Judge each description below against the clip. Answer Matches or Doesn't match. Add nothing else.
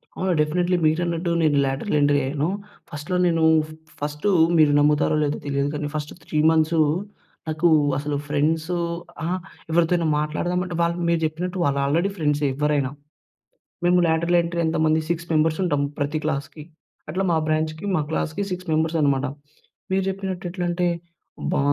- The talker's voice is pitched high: Doesn't match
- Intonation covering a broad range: Doesn't match